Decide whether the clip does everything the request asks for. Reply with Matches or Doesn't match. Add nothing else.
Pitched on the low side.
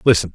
Matches